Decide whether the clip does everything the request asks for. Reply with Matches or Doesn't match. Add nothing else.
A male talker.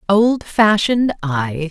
Doesn't match